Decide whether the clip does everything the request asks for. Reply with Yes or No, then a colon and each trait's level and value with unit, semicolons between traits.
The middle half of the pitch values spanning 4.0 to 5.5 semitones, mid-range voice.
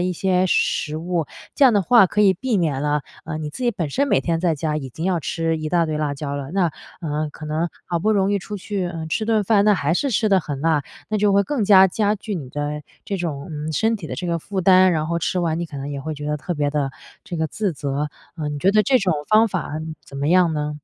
Yes: average, 4.6 semitones; medium, 170 Hz